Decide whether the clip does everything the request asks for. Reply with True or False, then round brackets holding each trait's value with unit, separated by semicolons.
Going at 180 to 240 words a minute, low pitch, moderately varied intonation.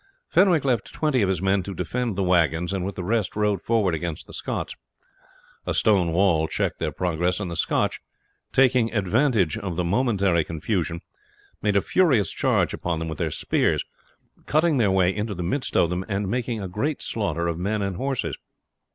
True (190 wpm; 100 Hz; 4.6 semitones)